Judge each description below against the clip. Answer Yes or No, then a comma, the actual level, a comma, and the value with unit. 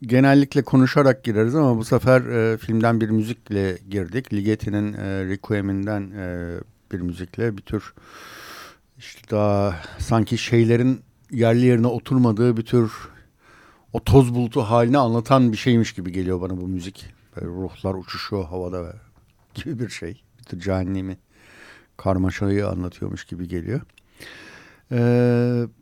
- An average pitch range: Yes, average, 4.1 semitones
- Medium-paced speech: Yes, average, 130 wpm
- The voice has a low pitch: Yes, low, 110 Hz